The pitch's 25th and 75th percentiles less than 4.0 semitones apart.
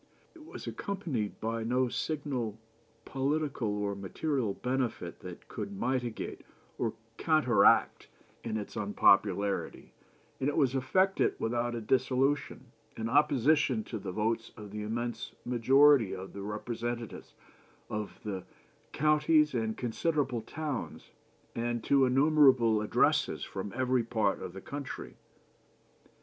No: average, 4.6 semitones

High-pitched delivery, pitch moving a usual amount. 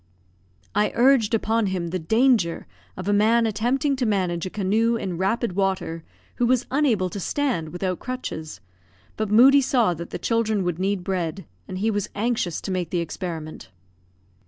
Yes: high, 205 Hz; average, 4.5 semitones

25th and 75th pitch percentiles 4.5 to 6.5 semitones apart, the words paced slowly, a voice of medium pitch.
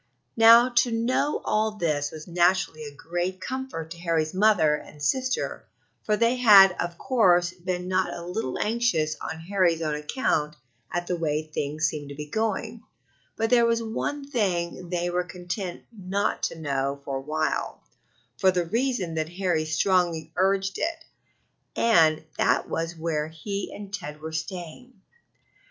No: average, 5.1 semitones; average, 160 wpm; medium, 175 Hz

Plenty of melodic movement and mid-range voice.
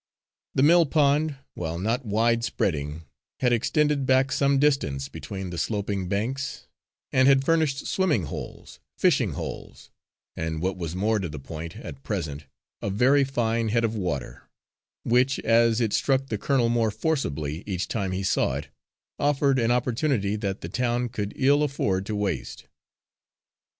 No: wide, 6.2 semitones; low, 115 Hz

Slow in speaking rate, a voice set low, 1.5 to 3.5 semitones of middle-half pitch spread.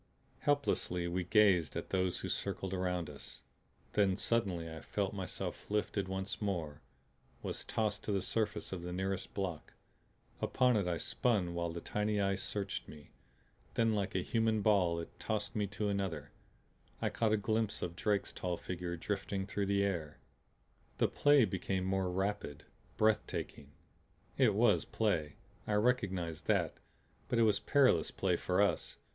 No: average, 160 wpm; very low, 95 Hz; average, 3.2 semitones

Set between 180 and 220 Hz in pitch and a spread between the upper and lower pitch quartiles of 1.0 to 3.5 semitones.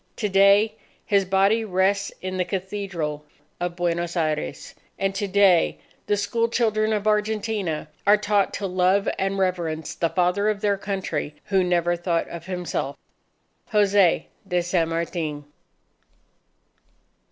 Yes: high, 190 Hz; average, 2.8 semitones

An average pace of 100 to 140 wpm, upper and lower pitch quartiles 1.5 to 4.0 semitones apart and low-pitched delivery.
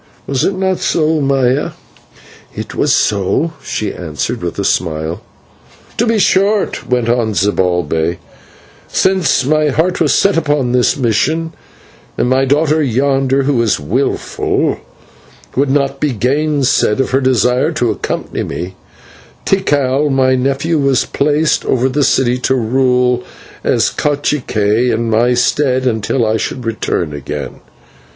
No: slow, 135 wpm; average, 4.4 semitones; low, 130 Hz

